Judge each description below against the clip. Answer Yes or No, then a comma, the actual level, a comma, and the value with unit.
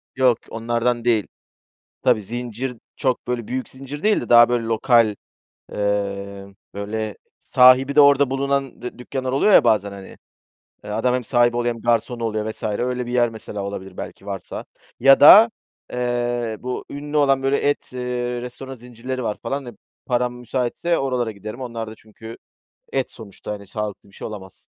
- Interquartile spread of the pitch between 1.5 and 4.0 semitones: Yes, average, 3.0 semitones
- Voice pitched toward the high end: No, low, 120 Hz